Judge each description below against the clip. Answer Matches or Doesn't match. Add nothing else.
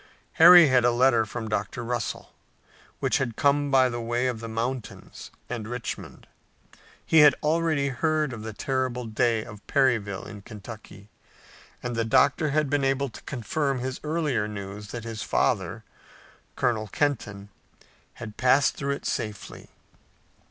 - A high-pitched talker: Doesn't match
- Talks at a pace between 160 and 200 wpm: Doesn't match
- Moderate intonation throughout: Matches